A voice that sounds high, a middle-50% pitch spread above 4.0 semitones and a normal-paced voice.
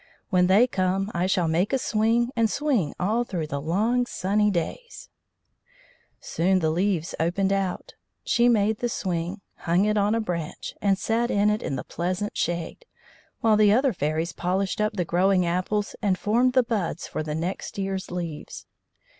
No: high, 195 Hz; average, 3.7 semitones; average, 175 wpm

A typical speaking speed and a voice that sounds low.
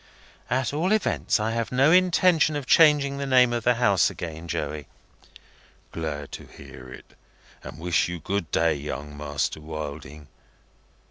Yes: average, 150 wpm; very low, 95 Hz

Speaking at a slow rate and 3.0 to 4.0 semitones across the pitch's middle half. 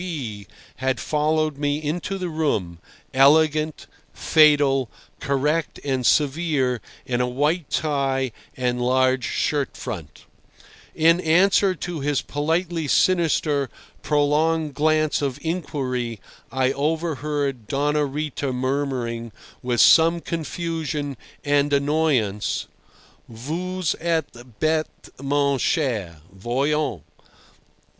Yes: slow, 100 wpm; average, 3.4 semitones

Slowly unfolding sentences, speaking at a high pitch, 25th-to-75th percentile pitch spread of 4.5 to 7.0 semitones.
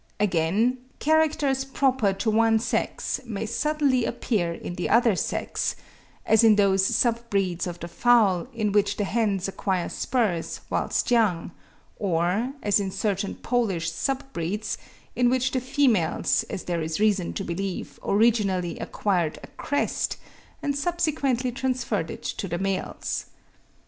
No: average, 145 wpm; high, 210 Hz; average, 4.8 semitones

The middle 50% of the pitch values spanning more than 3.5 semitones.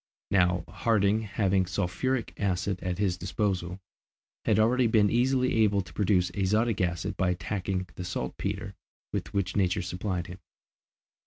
No: average, 2.9 semitones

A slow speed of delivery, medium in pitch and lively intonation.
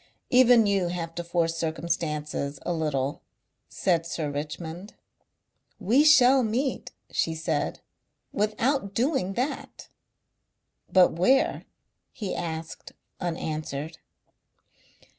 Yes: slow, 95 wpm; medium, 175 Hz; wide, 5.8 semitones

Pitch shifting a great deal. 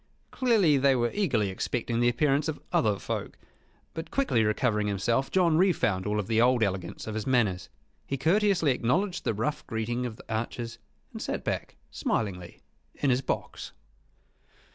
Yes: wide, 5.7 semitones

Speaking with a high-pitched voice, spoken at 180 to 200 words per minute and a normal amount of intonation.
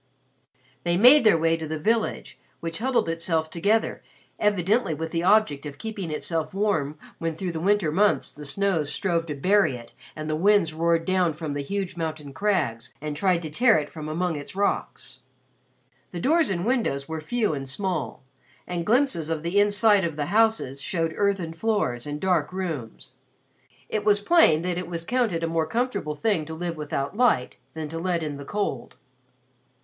No: medium, 170 Hz; average, 185 wpm; average, 4.8 semitones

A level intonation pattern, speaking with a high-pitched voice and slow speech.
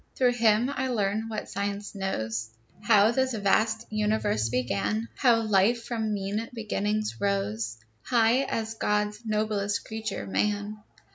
Yes: narrow, 2.3 semitones; high, 210 Hz; slow, 130 wpm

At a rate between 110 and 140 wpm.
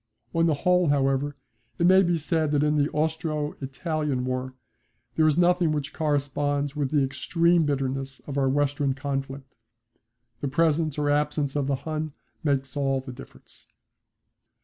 No: average, 155 wpm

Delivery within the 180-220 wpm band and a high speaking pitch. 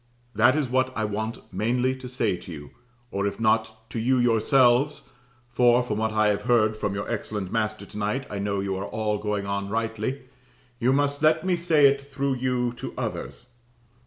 No: average, 195 wpm; low, 115 Hz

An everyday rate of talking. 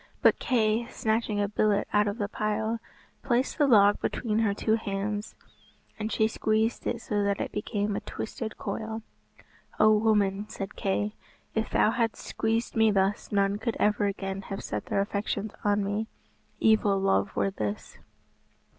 Yes: average, 165 wpm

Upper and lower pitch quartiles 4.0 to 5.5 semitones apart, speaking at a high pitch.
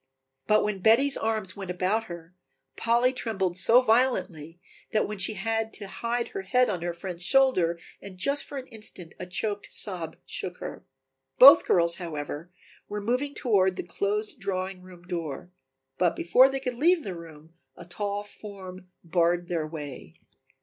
Yes: average, 4.5 semitones; high, 195 Hz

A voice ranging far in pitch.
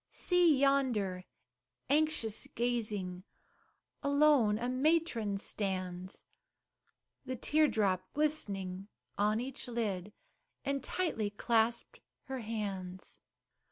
Yes: wide, 5.8 semitones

